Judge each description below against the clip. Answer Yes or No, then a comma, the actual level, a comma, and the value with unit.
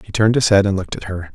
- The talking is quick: Yes, fast, 355 wpm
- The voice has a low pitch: Yes, low, 100 Hz